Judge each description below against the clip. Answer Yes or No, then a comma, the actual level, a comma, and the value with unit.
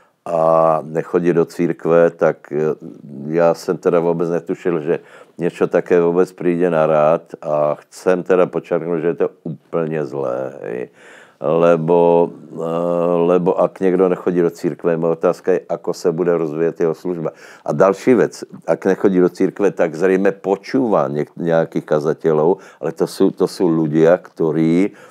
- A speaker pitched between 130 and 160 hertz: No, very low, 85 Hz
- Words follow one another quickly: No, average, 150 wpm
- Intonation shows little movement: Yes, narrow, 1.7 semitones